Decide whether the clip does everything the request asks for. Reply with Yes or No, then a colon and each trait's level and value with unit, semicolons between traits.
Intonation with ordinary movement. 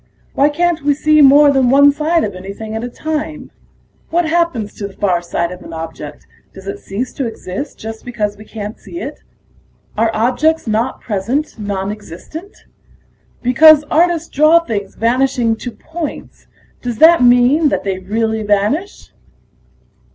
No: wide, 6.7 semitones